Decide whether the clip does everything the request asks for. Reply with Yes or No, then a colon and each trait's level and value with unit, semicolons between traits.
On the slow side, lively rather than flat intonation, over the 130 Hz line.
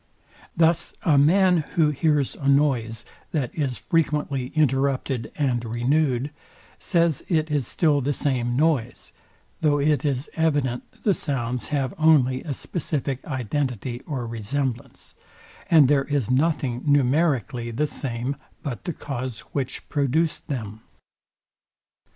No: slow, 125 wpm; average, 3.4 semitones; medium, 140 Hz